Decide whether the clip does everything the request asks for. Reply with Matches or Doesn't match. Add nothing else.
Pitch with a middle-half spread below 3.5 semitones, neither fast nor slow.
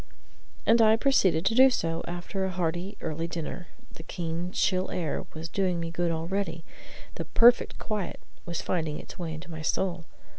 Matches